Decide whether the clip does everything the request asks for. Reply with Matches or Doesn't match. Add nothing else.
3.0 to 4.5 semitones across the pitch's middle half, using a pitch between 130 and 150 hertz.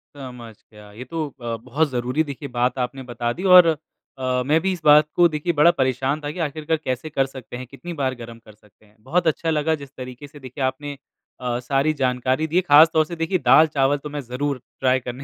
Matches